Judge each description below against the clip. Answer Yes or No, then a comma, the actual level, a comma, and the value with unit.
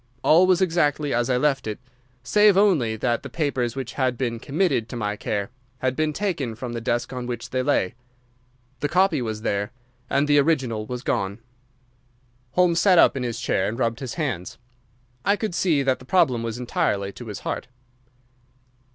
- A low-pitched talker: Yes, low, 130 Hz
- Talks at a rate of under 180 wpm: No, average, 185 wpm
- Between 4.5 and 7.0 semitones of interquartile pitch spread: Yes, average, 5.1 semitones